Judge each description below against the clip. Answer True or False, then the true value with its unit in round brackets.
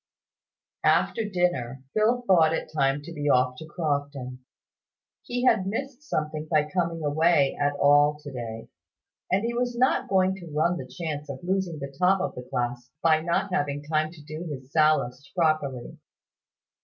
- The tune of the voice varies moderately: True (4.2 semitones)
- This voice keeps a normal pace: True (165 wpm)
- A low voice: False (155 Hz)